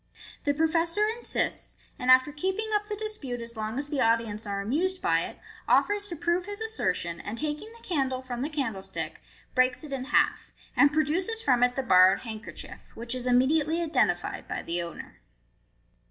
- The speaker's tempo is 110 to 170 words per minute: No, average, 180 wpm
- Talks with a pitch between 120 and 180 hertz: No, very high, 285 Hz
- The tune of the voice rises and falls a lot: Yes, wide, 6.6 semitones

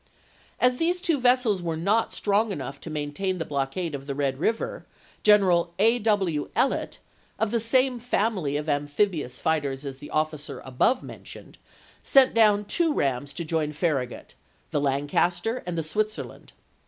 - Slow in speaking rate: No, average, 160 wpm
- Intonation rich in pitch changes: Yes, wide, 7.4 semitones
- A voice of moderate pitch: Yes, medium, 175 Hz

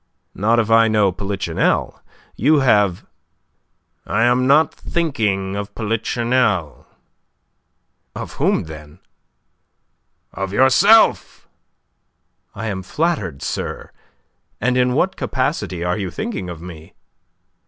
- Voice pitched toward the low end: Yes, low, 110 Hz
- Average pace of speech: No, slow, 105 wpm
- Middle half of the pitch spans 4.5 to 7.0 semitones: Yes, average, 5.3 semitones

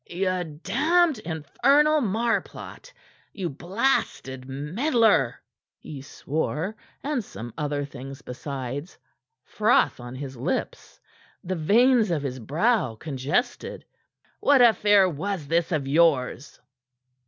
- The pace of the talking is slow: Yes, slow, 105 wpm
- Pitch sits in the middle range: Yes, medium, 165 Hz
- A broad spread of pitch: Yes, wide, 8.2 semitones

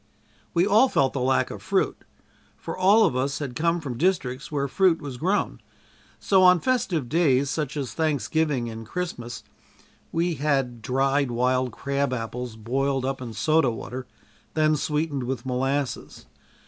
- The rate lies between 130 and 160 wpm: Yes, average, 155 wpm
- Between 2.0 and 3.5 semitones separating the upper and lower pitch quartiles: No, average, 4.2 semitones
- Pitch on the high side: No, medium, 140 Hz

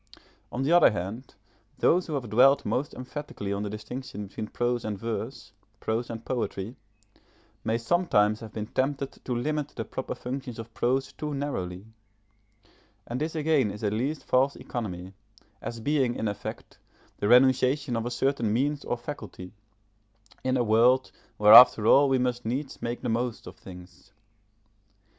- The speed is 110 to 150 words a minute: No, average, 160 wpm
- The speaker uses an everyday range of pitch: Yes, average, 3.9 semitones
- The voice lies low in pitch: Yes, low, 120 Hz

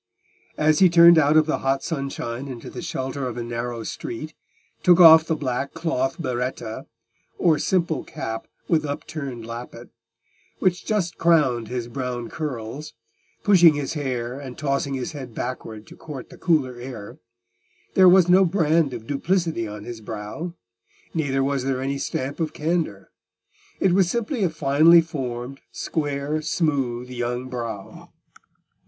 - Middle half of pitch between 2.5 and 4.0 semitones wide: No, average, 4.8 semitones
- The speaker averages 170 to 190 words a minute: No, average, 150 wpm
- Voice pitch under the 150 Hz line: Yes, medium, 140 Hz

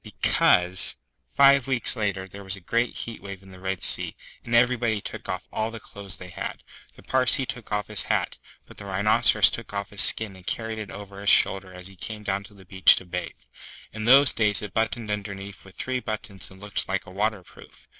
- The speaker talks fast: Yes, fast, 215 wpm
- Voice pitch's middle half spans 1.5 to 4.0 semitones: Yes, average, 2.7 semitones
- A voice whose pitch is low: Yes, low, 100 Hz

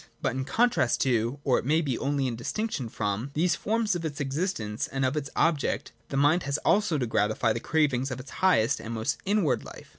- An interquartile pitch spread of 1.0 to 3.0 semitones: No, wide, 5.5 semitones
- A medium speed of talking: No, fast, 215 wpm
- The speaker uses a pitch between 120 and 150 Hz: Yes, medium, 140 Hz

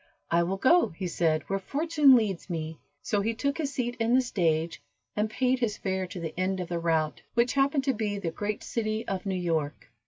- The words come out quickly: Yes, fast, 220 wpm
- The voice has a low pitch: No, high, 200 Hz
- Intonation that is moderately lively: No, wide, 6.3 semitones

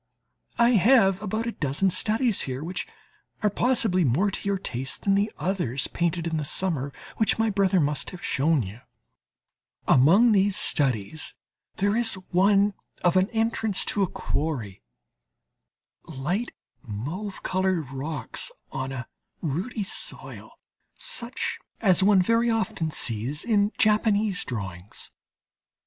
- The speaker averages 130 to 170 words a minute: Yes, slow, 135 wpm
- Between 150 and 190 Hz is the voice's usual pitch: Yes, medium, 185 Hz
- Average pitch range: No, wide, 6.7 semitones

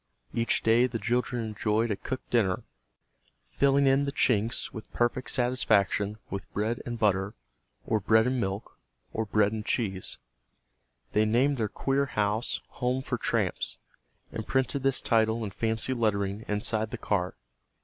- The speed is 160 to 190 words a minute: No, average, 150 wpm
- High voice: No, low, 110 Hz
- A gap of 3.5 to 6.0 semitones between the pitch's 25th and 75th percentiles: No, average, 3.0 semitones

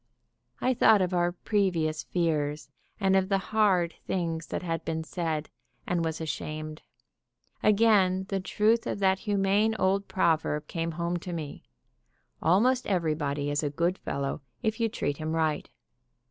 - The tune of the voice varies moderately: Yes, average, 3.7 semitones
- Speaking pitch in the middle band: Yes, medium, 175 Hz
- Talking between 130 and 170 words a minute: Yes, average, 150 wpm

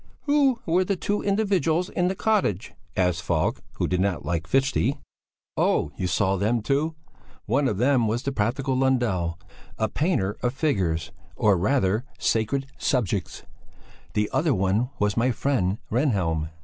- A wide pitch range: Yes, wide, 7.0 semitones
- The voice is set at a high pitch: No, low, 120 Hz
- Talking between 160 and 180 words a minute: No, average, 150 wpm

